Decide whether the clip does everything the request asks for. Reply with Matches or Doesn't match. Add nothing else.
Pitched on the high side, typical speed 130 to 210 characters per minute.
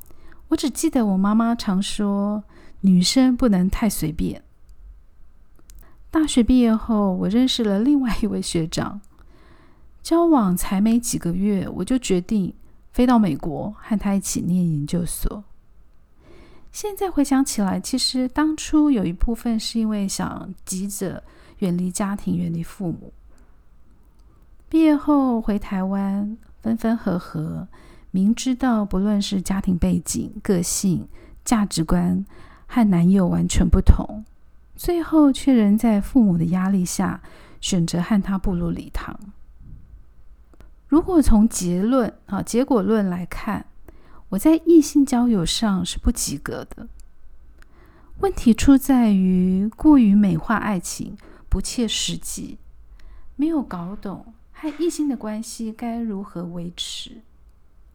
Matches